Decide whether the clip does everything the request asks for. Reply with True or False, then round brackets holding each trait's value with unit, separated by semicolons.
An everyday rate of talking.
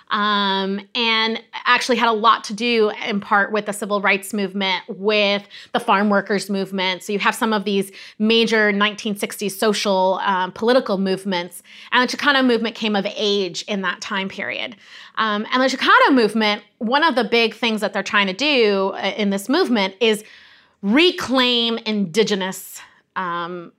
True (165 wpm)